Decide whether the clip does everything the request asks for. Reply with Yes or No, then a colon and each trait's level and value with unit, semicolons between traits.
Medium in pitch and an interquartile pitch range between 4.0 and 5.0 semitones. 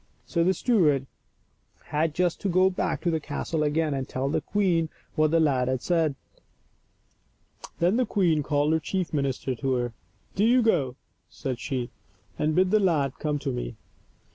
Yes: medium, 155 Hz; average, 4.7 semitones